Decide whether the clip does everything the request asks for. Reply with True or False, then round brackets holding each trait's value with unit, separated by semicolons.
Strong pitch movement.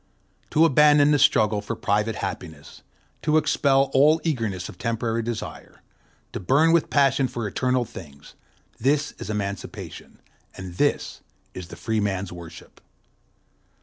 True (6.1 semitones)